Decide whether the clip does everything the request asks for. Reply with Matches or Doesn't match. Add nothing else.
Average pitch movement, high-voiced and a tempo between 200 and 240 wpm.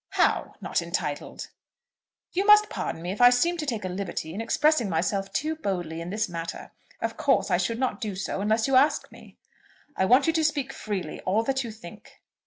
Doesn't match